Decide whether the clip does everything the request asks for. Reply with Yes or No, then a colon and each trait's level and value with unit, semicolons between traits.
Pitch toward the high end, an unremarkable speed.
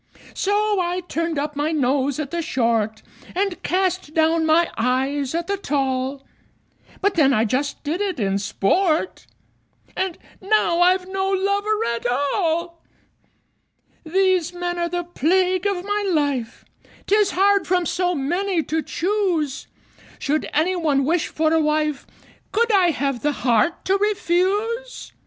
Yes: very high, 340 Hz; average, 145 wpm